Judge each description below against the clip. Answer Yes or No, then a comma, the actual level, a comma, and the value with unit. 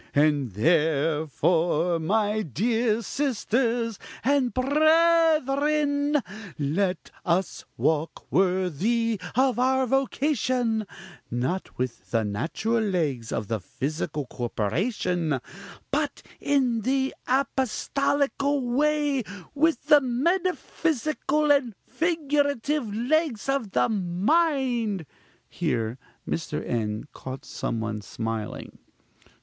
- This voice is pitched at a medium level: No, high, 230 Hz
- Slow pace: Yes, slow, 90 wpm